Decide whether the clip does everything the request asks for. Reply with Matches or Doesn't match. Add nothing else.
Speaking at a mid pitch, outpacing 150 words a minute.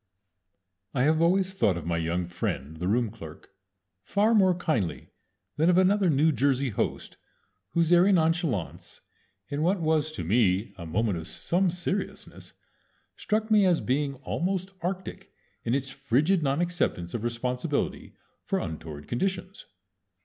Doesn't match